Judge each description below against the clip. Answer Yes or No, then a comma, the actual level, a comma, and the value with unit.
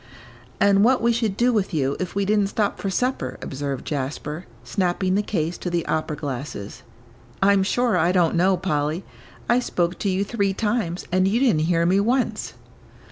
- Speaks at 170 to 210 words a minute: Yes, average, 185 wpm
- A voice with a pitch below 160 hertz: No, medium, 185 Hz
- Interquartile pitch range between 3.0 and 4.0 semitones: No, average, 4.5 semitones